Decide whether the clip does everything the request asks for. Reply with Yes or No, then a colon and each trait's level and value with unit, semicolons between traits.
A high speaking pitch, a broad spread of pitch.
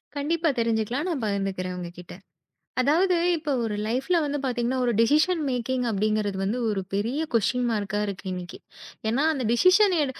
Yes: high, 240 Hz; wide, 6.1 semitones